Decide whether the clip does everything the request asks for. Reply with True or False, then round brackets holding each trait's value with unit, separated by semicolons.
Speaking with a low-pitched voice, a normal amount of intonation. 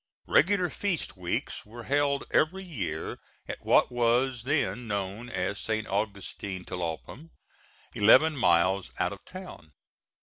False (115 Hz; 7.0 semitones)